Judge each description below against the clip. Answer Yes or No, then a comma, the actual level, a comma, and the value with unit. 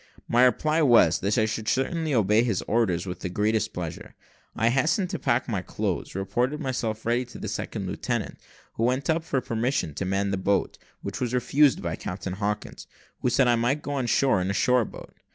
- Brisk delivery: Yes, fast, 210 wpm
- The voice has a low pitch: Yes, low, 115 Hz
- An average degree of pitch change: Yes, average, 4.7 semitones